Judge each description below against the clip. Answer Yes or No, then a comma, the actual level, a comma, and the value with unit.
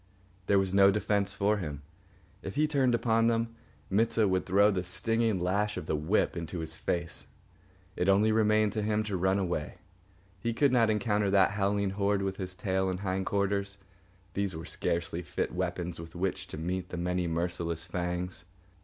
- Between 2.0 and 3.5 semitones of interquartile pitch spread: Yes, average, 2.8 semitones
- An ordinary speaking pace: Yes, average, 180 wpm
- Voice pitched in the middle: No, very low, 95 Hz